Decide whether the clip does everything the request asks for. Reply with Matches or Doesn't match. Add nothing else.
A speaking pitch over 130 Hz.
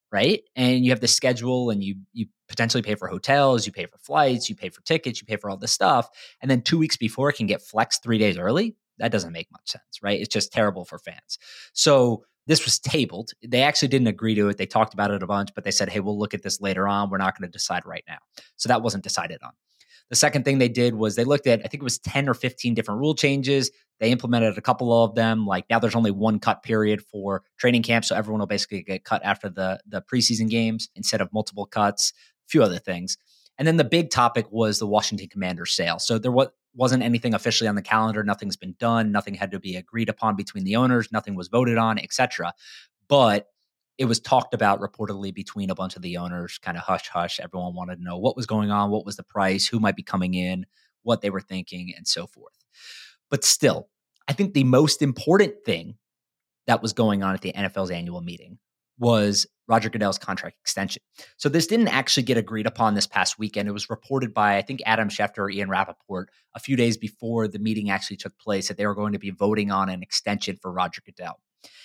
Doesn't match